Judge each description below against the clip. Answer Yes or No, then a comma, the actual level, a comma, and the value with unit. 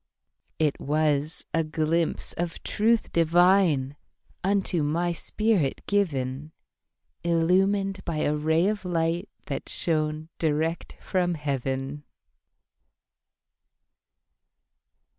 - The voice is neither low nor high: Yes, medium, 165 Hz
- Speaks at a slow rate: Yes, slow, 75 wpm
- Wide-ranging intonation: No, average, 3.2 semitones